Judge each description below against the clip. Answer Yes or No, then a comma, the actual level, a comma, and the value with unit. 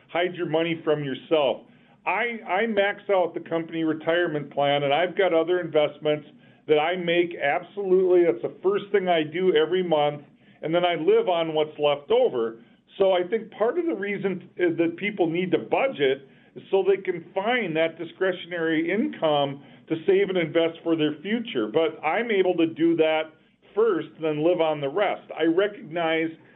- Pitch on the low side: No, medium, 175 Hz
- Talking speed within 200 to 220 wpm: No, average, 185 wpm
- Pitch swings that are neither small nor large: Yes, average, 3.4 semitones